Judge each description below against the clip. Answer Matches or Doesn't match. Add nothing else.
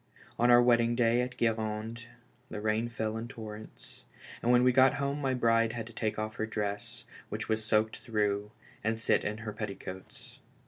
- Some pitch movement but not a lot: Doesn't match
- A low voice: Matches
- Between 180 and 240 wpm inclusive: Matches